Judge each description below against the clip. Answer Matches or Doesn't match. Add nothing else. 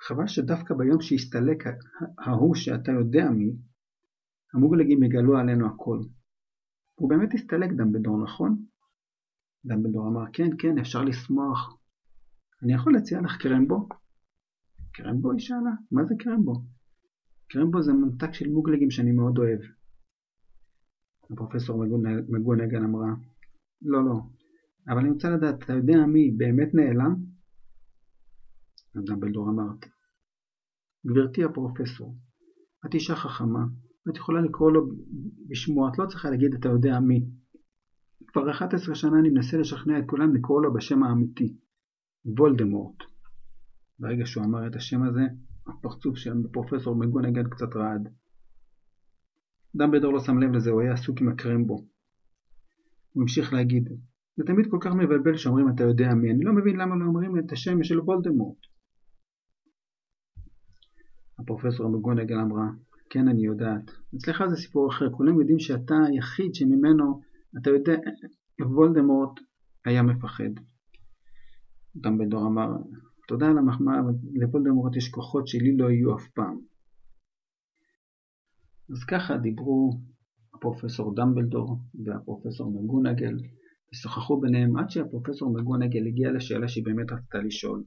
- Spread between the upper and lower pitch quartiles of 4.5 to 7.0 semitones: Matches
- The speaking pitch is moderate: Doesn't match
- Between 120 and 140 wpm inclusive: Matches